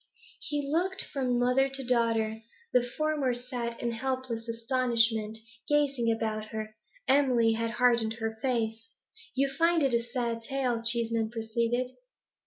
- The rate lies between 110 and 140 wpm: Yes, slow, 135 wpm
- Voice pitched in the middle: No, high, 240 Hz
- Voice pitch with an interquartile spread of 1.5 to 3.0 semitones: Yes, narrow, 2.6 semitones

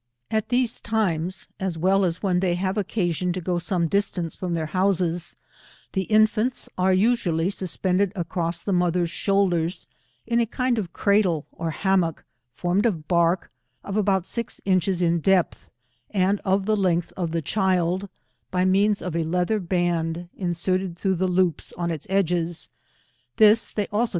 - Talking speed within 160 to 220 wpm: Yes, average, 170 wpm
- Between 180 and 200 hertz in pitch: Yes, medium, 185 Hz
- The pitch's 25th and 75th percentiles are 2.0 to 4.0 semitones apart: Yes, narrow, 2.6 semitones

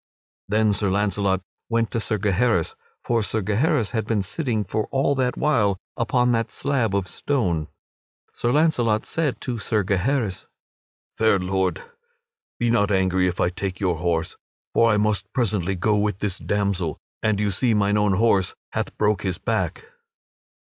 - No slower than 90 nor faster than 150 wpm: No, average, 165 wpm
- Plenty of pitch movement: No, average, 3.3 semitones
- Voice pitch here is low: Yes, low, 105 Hz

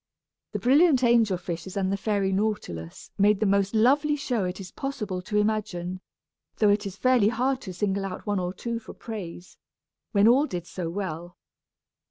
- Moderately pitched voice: No, high, 205 Hz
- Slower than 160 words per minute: No, average, 180 wpm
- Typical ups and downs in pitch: Yes, average, 3.8 semitones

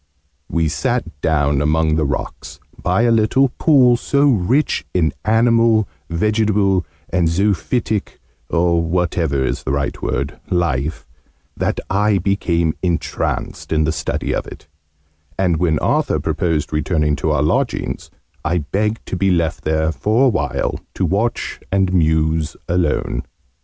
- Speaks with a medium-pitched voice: No, very low, 85 Hz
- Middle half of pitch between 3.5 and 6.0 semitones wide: Yes, average, 5.1 semitones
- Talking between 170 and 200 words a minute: No, average, 140 wpm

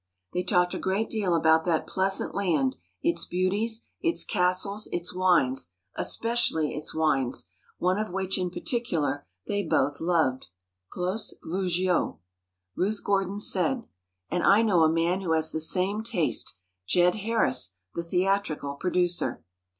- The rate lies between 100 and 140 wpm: Yes, slow, 135 wpm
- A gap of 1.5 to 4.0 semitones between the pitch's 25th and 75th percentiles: Yes, average, 3.7 semitones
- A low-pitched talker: No, medium, 180 Hz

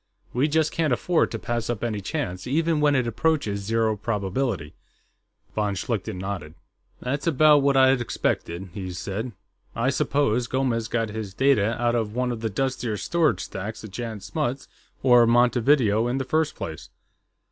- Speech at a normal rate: Yes, average, 165 wpm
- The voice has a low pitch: Yes, low, 120 Hz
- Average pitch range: Yes, average, 4.4 semitones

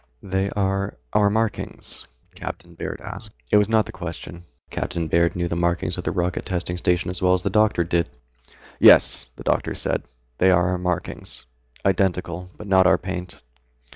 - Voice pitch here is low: Yes, very low, 90 Hz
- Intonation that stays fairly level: Yes, narrow, 1.8 semitones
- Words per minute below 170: No, average, 175 wpm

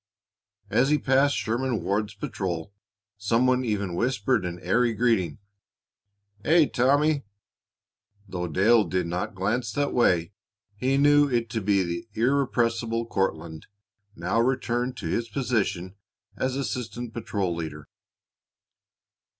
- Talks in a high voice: No, low, 115 Hz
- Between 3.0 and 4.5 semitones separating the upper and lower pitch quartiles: No, average, 5.3 semitones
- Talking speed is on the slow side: Yes, slow, 120 wpm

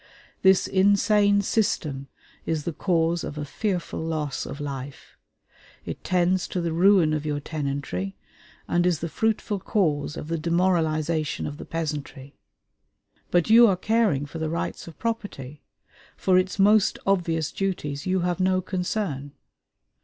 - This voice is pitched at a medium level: Yes, medium, 170 Hz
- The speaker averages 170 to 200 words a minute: No, average, 145 wpm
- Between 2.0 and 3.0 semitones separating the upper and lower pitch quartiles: No, average, 4.2 semitones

